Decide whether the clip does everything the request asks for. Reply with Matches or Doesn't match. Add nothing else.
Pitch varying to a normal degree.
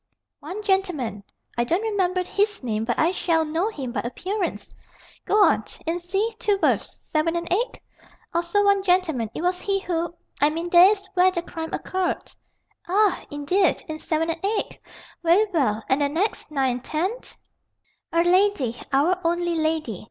Matches